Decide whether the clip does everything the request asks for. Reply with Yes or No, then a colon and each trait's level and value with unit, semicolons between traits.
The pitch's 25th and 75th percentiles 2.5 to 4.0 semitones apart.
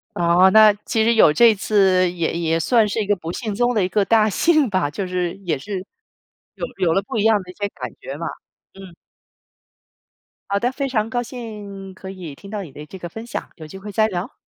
Yes: average, 3.5 semitones